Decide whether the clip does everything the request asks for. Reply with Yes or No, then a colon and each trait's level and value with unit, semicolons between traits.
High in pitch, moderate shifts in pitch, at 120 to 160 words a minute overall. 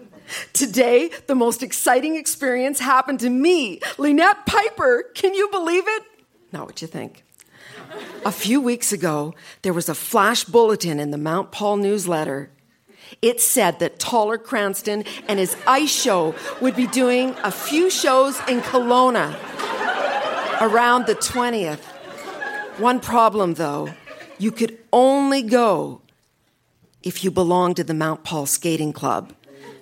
No: high, 235 Hz; wide, 6.2 semitones; slow, 135 wpm